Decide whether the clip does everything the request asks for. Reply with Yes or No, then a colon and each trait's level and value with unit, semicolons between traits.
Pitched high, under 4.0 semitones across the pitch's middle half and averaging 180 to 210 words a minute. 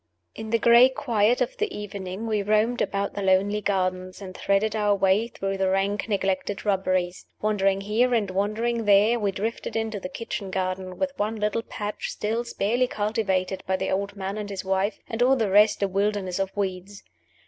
Yes: high, 205 Hz; narrow, 2.4 semitones; average, 190 wpm